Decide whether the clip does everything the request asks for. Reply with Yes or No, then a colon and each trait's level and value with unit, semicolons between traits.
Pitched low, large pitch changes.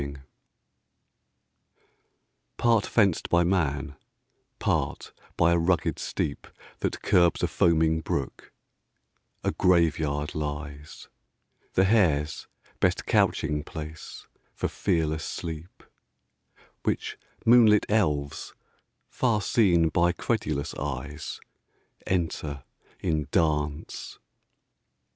No: very low, 80 Hz; average, 3.8 semitones